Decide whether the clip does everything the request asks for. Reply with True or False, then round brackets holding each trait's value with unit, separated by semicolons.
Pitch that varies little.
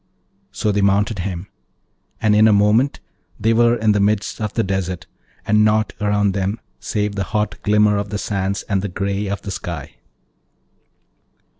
True (1.4 semitones)